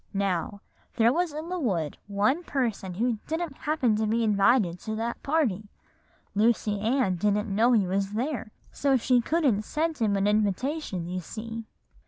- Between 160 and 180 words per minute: Yes, average, 165 wpm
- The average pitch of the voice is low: No, high, 225 Hz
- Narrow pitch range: No, average, 4.9 semitones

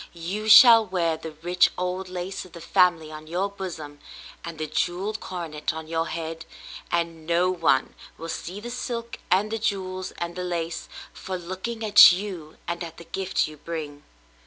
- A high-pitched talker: No, medium, 175 Hz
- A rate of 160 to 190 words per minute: Yes, average, 180 wpm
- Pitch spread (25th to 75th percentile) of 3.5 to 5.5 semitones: No, average, 2.7 semitones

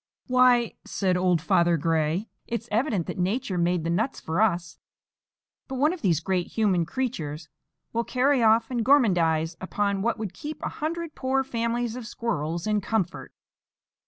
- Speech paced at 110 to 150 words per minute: No, average, 160 wpm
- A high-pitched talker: Yes, high, 210 Hz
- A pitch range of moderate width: No, wide, 6.1 semitones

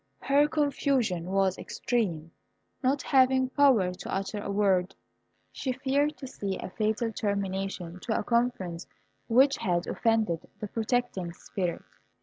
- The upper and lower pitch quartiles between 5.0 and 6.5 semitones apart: Yes, wide, 5.6 semitones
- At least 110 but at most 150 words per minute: Yes, slow, 135 wpm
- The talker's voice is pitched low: No, high, 215 Hz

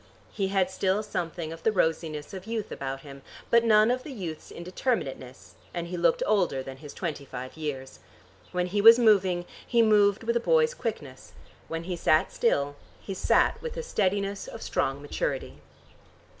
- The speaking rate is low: No, average, 170 wpm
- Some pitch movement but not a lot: No, wide, 5.8 semitones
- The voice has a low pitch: No, medium, 185 Hz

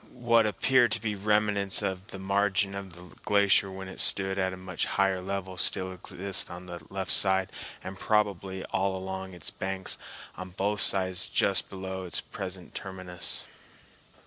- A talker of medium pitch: No, very low, 95 Hz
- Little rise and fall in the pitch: Yes, narrow, 1.1 semitones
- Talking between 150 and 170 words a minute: Yes, average, 165 wpm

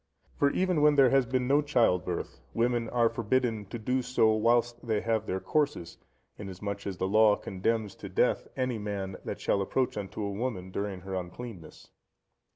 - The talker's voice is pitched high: No, low, 110 Hz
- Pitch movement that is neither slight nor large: Yes, average, 4.1 semitones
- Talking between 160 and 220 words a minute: Yes, average, 180 wpm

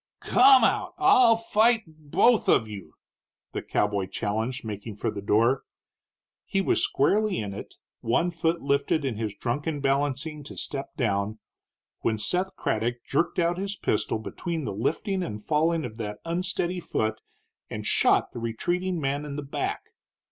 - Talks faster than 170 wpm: No, average, 160 wpm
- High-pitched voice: No, medium, 140 Hz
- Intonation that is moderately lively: No, wide, 8.1 semitones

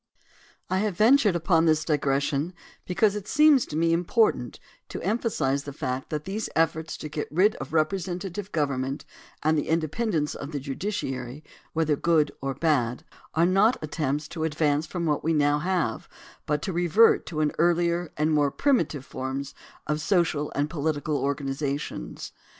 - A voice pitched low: No, medium, 155 Hz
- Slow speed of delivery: No, average, 160 wpm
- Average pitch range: Yes, average, 3.6 semitones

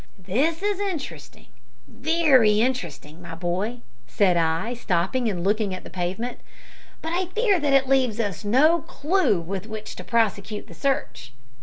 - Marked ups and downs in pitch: Yes, wide, 7.5 semitones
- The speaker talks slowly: No, average, 155 wpm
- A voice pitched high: Yes, high, 225 Hz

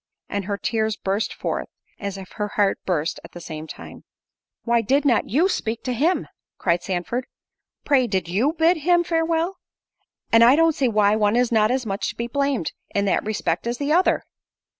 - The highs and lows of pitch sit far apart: Yes, wide, 5.9 semitones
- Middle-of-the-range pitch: No, high, 230 Hz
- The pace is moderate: Yes, average, 190 wpm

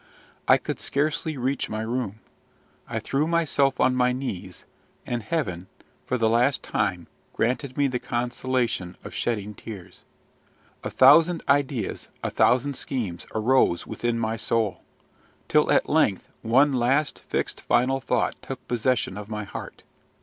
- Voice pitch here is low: Yes, low, 125 Hz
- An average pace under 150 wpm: Yes, average, 140 wpm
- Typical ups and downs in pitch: Yes, average, 3.9 semitones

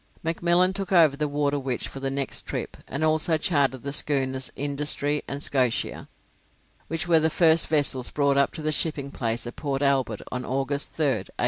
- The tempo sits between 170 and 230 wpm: Yes, average, 185 wpm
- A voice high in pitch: No, medium, 140 Hz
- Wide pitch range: No, narrow, 2.6 semitones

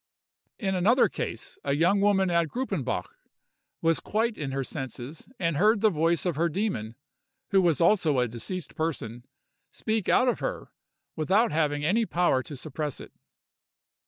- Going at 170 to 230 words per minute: No, average, 160 wpm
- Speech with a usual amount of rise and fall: No, wide, 5.7 semitones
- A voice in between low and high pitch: Yes, medium, 170 Hz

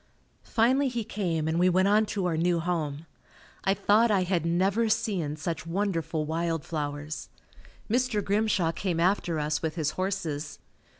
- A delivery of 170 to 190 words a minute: No, average, 160 wpm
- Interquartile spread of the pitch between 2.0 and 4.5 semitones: Yes, average, 4.2 semitones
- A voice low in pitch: No, medium, 175 Hz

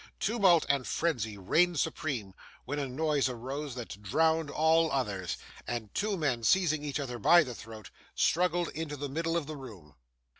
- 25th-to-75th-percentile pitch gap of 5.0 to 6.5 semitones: Yes, average, 5.3 semitones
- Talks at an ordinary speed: Yes, average, 165 wpm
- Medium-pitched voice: Yes, medium, 145 Hz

